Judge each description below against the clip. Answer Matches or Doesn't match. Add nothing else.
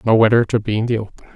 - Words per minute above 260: Matches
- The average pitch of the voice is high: Doesn't match